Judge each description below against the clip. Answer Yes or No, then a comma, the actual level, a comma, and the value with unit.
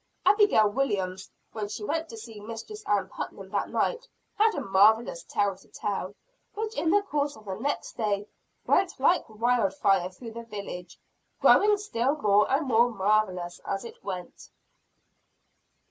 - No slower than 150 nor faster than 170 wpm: Yes, average, 155 wpm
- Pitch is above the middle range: Yes, high, 220 Hz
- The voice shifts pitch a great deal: Yes, wide, 6.3 semitones